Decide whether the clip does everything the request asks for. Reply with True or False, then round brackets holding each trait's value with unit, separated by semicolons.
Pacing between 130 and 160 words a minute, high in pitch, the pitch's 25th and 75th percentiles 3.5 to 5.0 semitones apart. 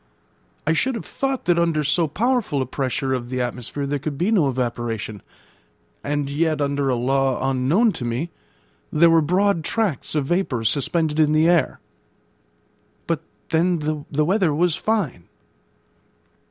False (155 wpm; 150 Hz; 4.4 semitones)